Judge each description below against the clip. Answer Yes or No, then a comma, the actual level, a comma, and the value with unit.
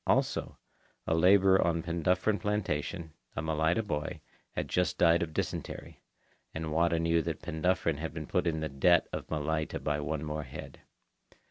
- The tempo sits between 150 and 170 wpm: Yes, average, 160 wpm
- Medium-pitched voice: No, very low, 80 Hz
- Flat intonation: Yes, narrow, 2.1 semitones